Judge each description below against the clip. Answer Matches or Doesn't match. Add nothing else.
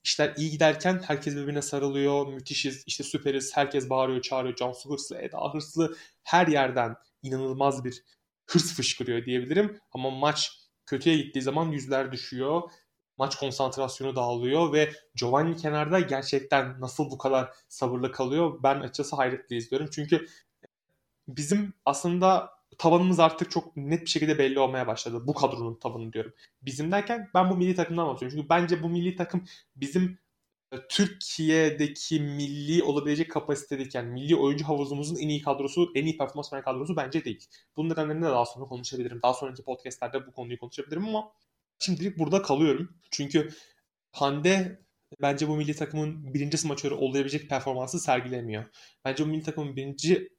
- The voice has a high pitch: Doesn't match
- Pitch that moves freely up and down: Doesn't match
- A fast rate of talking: Matches